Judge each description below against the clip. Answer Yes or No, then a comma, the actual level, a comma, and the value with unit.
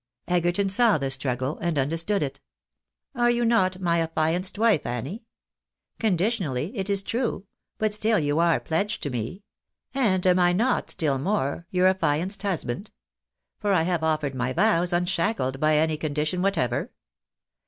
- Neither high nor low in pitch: Yes, medium, 175 Hz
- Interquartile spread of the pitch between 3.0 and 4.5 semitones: No, average, 4.9 semitones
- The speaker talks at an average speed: Yes, average, 155 wpm